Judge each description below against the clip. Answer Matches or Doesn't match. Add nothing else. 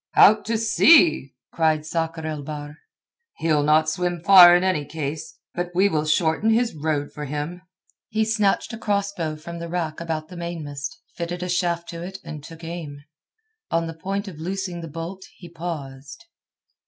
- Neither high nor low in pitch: Matches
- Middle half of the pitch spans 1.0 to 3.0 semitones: Matches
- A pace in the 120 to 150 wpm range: Doesn't match